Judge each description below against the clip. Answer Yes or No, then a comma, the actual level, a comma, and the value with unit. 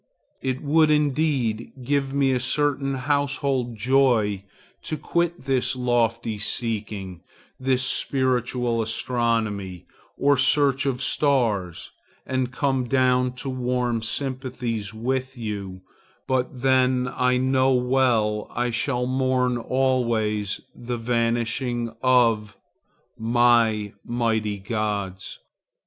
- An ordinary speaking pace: No, slow, 100 wpm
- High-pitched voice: No, low, 125 Hz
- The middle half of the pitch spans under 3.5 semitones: Yes, narrow, 2.6 semitones